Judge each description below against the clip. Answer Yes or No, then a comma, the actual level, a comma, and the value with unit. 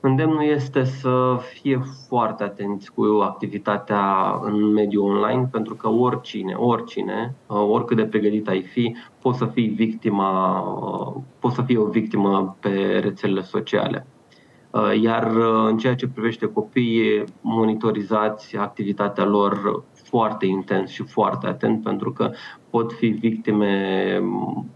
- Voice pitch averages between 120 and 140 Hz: No, low, 110 Hz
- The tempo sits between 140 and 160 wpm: No, average, 120 wpm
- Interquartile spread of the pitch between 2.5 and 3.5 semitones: Yes, average, 3.2 semitones